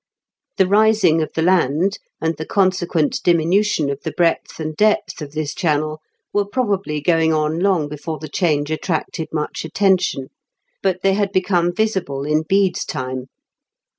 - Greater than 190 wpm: No, average, 155 wpm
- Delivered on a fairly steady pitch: No, average, 3.9 semitones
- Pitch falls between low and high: Yes, medium, 165 Hz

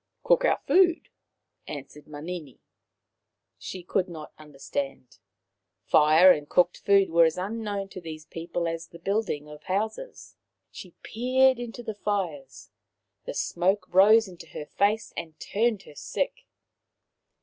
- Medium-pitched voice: Yes, medium, 180 Hz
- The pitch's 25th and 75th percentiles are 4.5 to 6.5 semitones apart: Yes, average, 5.3 semitones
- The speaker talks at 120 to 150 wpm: Yes, average, 140 wpm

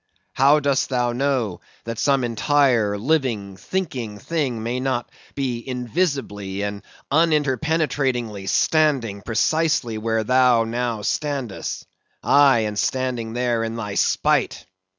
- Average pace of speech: No, slow, 115 wpm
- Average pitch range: Yes, average, 3.9 semitones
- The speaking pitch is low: Yes, low, 125 Hz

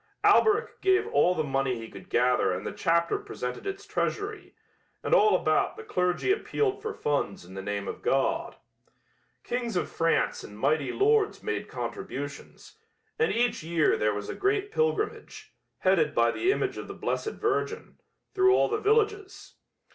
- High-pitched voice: Yes, very high, 355 Hz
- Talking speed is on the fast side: No, average, 165 wpm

